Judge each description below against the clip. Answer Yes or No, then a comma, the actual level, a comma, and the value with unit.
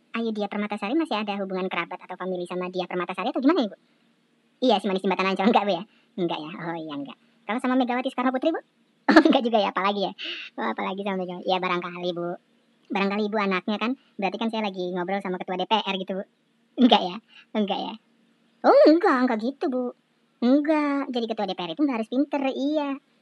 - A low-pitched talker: No, high, 215 Hz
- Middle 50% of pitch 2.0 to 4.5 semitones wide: No, wide, 5.5 semitones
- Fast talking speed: Yes, fast, 215 wpm